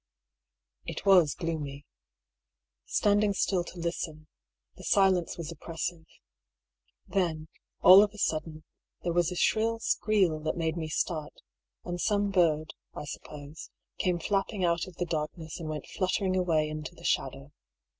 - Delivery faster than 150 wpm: No, average, 145 wpm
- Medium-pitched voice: Yes, medium, 170 Hz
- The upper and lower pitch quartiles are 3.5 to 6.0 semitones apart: No, average, 3.1 semitones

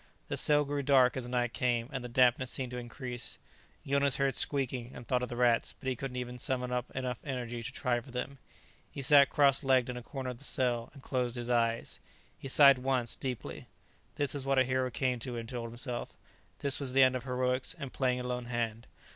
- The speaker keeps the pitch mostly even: Yes, narrow, 1.6 semitones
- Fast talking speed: Yes, fast, 220 wpm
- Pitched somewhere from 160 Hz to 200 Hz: No, low, 125 Hz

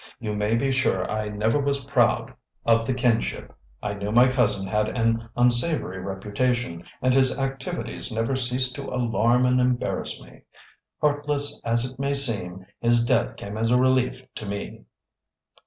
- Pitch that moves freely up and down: No, average, 3.4 semitones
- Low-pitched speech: Yes, low, 120 Hz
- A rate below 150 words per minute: No, average, 160 wpm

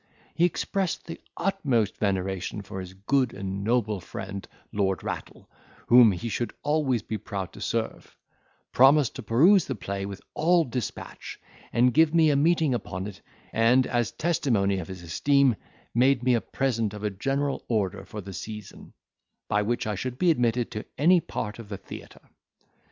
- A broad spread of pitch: Yes, wide, 5.7 semitones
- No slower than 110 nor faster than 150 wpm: No, average, 175 wpm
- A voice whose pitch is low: Yes, low, 115 Hz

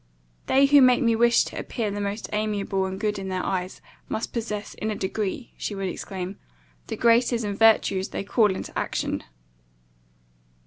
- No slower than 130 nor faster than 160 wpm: No, average, 175 wpm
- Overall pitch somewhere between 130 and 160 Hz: No, high, 210 Hz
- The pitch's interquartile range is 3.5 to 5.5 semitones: No, average, 3.0 semitones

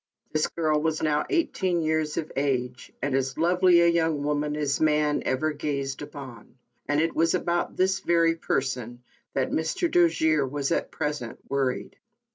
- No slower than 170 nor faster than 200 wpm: No, average, 160 wpm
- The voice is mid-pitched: Yes, medium, 150 Hz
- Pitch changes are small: No, average, 3.1 semitones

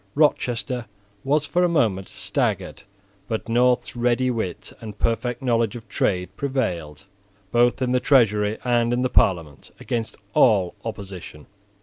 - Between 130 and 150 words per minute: Yes, slow, 135 wpm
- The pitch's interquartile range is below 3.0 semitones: No, average, 3.5 semitones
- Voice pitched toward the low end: Yes, low, 115 Hz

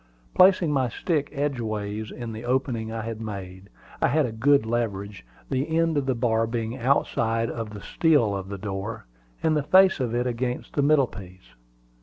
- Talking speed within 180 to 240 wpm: Yes, average, 185 wpm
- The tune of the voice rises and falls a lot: No, average, 4.4 semitones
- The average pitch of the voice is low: Yes, low, 115 Hz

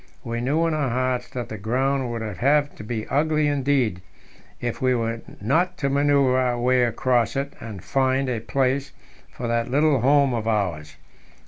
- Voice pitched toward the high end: No, low, 130 Hz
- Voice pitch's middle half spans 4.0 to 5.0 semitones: No, average, 3.2 semitones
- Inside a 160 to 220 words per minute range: Yes, average, 180 wpm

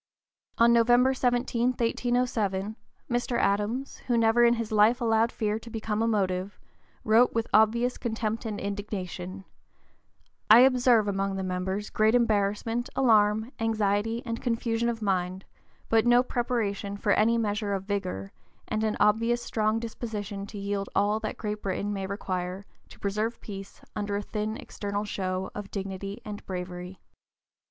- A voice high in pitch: Yes, high, 215 Hz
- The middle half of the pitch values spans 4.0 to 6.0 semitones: No, narrow, 2.6 semitones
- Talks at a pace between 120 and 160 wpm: Yes, average, 155 wpm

